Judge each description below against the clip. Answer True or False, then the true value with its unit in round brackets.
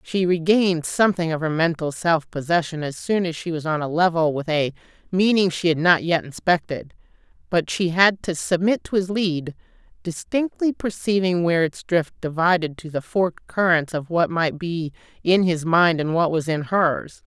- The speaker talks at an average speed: True (185 wpm)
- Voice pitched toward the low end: False (170 Hz)